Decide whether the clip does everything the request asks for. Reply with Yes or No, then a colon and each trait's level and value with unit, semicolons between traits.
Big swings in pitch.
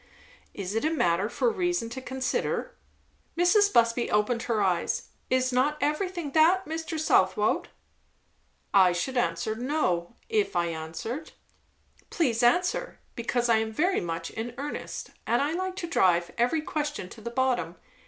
Yes: wide, 7.1 semitones